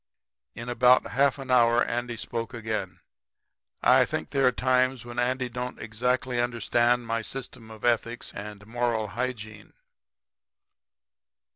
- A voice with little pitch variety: Yes, narrow, 1.9 semitones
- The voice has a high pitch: No, low, 120 Hz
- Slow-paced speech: Yes, slow, 130 wpm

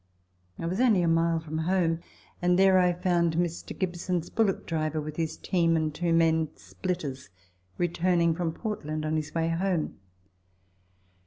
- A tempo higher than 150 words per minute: Yes, average, 160 wpm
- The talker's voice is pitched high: No, medium, 165 Hz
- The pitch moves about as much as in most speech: No, narrow, 2.0 semitones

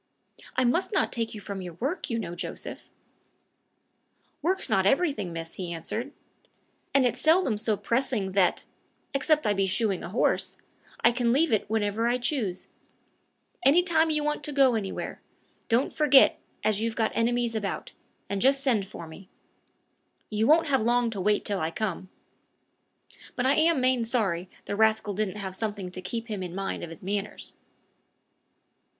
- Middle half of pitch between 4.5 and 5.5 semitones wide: Yes, average, 5.1 semitones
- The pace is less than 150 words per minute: No, average, 170 wpm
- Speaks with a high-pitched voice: Yes, high, 220 Hz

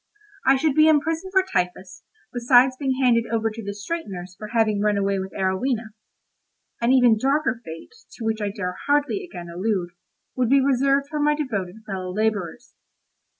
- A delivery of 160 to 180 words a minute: Yes, average, 170 wpm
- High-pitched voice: Yes, high, 230 Hz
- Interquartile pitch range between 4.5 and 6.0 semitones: Yes, wide, 5.6 semitones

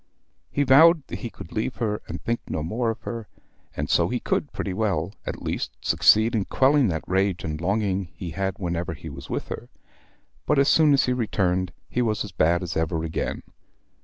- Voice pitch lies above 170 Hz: No, low, 100 Hz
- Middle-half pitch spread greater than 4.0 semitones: Yes, wide, 5.5 semitones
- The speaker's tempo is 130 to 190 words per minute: No, fast, 205 wpm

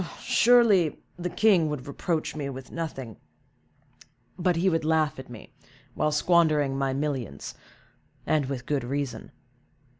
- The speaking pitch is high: No, medium, 150 Hz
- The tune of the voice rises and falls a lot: No, average, 4.0 semitones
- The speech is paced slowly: Yes, slow, 130 wpm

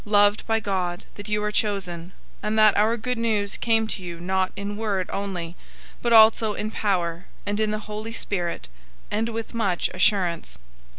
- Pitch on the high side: Yes, high, 205 Hz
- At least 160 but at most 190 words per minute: Yes, average, 185 wpm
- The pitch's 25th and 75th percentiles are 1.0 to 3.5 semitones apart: Yes, average, 2.9 semitones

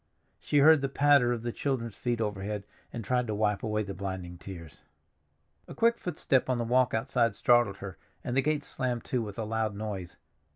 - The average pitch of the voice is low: Yes, low, 115 Hz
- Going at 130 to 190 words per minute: No, average, 200 wpm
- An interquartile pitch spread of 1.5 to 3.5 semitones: No, average, 3.9 semitones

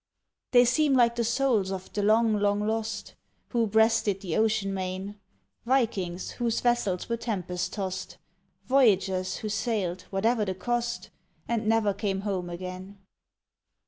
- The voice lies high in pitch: Yes, high, 210 Hz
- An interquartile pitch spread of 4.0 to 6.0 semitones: No, average, 3.6 semitones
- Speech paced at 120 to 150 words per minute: Yes, average, 140 wpm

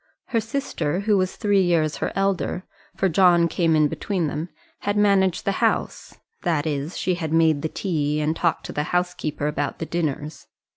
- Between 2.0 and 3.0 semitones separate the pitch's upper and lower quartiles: No, average, 3.8 semitones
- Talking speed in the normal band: Yes, average, 185 wpm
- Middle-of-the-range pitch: Yes, medium, 170 Hz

